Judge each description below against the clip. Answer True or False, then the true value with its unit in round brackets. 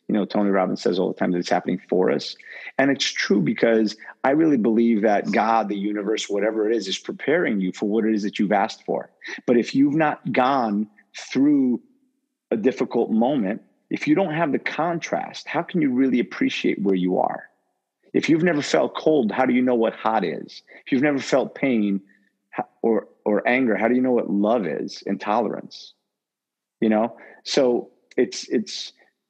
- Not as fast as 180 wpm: False (195 wpm)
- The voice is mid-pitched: False (110 Hz)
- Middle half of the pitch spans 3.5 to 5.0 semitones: True (4.7 semitones)